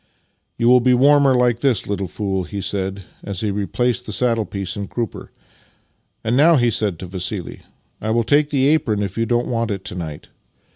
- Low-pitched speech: Yes, low, 110 Hz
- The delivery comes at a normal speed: No, fast, 220 wpm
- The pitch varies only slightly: No, average, 4.0 semitones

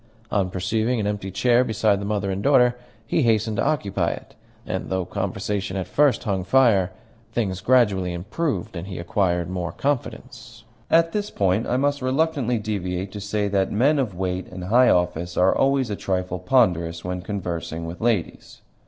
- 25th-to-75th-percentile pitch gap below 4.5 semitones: No, average, 4.9 semitones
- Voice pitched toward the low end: Yes, low, 100 Hz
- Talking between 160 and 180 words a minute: Yes, average, 175 wpm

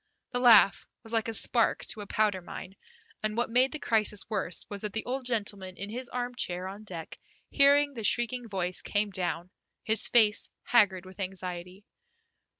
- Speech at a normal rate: Yes, average, 175 wpm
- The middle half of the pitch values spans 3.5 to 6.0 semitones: Yes, average, 4.1 semitones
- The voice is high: Yes, high, 210 Hz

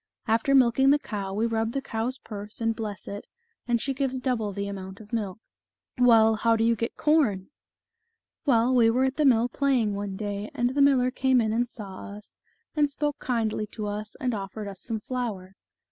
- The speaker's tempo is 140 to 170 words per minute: No, fast, 205 wpm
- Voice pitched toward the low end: No, high, 230 Hz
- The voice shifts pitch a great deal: No, average, 3.8 semitones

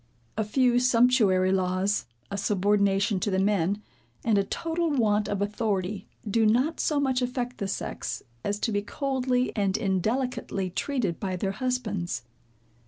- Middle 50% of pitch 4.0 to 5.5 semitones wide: Yes, average, 4.4 semitones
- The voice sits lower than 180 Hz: No, high, 210 Hz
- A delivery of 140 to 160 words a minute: Yes, average, 150 wpm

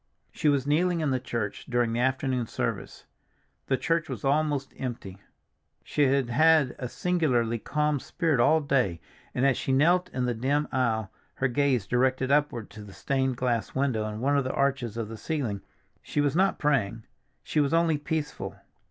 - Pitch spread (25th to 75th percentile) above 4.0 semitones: No, average, 3.7 semitones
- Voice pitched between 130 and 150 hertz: Yes, low, 135 Hz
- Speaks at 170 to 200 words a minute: Yes, average, 180 wpm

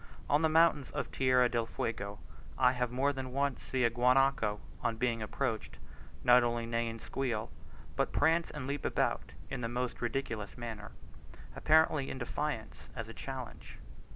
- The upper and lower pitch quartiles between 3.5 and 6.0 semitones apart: No, average, 2.9 semitones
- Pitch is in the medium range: No, low, 125 Hz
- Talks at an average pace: Yes, average, 165 wpm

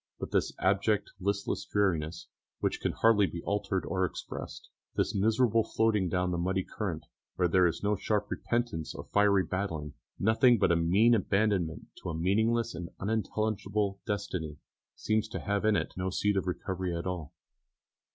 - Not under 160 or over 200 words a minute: Yes, average, 165 wpm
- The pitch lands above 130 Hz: No, low, 100 Hz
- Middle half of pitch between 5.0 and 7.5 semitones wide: No, average, 2.9 semitones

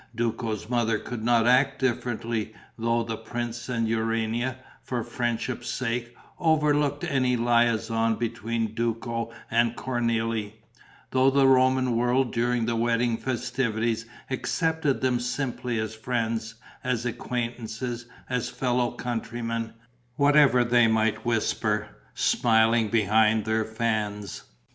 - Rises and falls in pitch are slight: Yes, narrow, 1.7 semitones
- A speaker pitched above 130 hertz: No, low, 120 Hz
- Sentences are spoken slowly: Yes, slow, 115 wpm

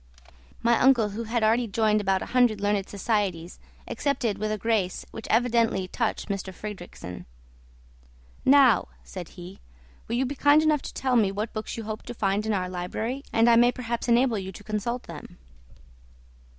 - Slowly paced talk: No, average, 175 wpm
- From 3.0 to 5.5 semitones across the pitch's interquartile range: Yes, average, 3.3 semitones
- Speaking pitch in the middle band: No, high, 220 Hz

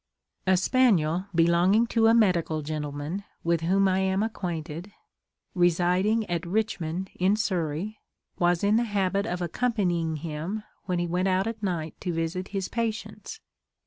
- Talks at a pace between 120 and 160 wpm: Yes, average, 145 wpm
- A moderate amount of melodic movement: Yes, average, 3.6 semitones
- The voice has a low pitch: No, medium, 185 Hz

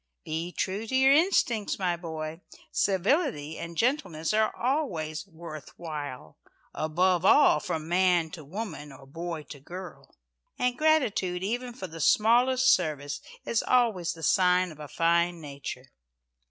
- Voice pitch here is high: No, medium, 175 Hz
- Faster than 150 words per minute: No, average, 140 wpm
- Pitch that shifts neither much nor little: No, wide, 6.1 semitones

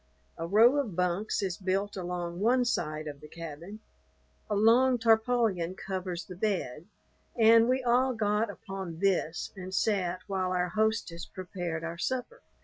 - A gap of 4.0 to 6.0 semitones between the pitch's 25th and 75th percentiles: Yes, average, 4.4 semitones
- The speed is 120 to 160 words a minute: Yes, average, 150 wpm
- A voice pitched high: Yes, high, 195 Hz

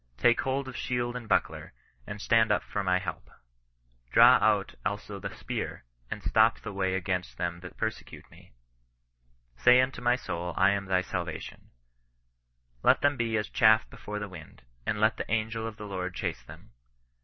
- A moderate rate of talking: Yes, average, 180 wpm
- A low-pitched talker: Yes, low, 105 Hz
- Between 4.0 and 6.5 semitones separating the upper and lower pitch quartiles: No, average, 3.6 semitones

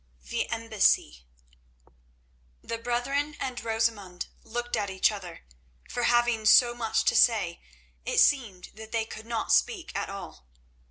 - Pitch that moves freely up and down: No, average, 3.3 semitones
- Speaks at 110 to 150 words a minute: Yes, average, 140 wpm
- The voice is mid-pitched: No, high, 225 Hz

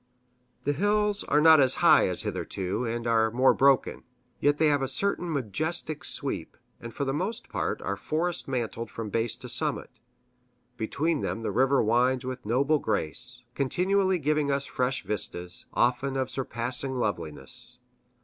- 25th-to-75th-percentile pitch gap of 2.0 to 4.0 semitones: No, average, 4.4 semitones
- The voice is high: No, low, 130 Hz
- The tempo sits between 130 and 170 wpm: Yes, average, 160 wpm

